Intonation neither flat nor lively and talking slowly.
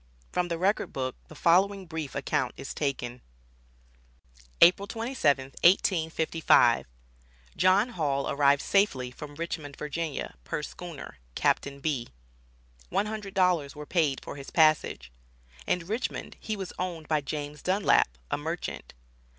Yes: average, 4.6 semitones; slow, 130 wpm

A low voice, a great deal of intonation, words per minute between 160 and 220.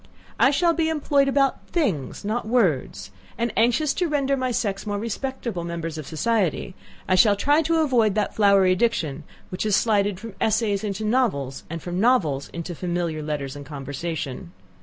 No: high, 205 Hz; wide, 6.8 semitones; average, 170 wpm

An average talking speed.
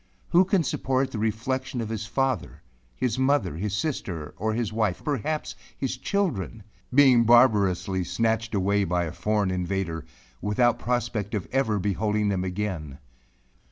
Yes: average, 150 wpm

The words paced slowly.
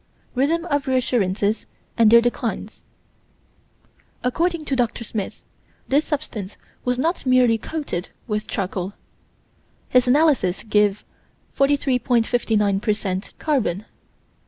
Yes: slow, 105 wpm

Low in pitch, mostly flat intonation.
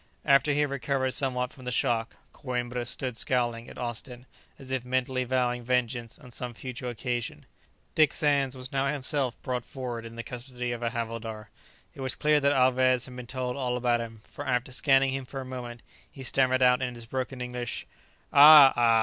Yes: low, 125 Hz; narrow, 1.7 semitones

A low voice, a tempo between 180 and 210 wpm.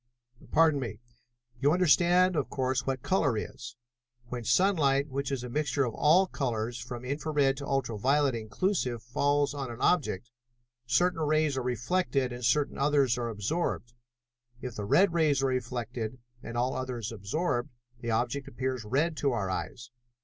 No: low, 130 Hz; average, 165 wpm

